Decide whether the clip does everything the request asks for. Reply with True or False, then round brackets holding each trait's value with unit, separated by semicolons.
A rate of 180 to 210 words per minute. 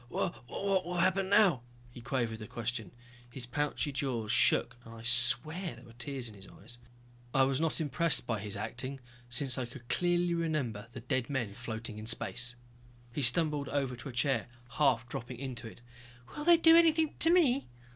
True (185 wpm)